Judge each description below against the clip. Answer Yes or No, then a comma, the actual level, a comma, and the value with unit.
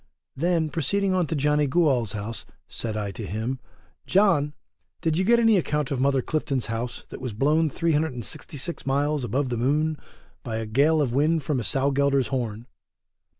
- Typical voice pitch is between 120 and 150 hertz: Yes, medium, 140 Hz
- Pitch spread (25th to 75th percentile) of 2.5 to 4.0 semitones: No, average, 4.4 semitones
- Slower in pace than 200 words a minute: Yes, average, 175 wpm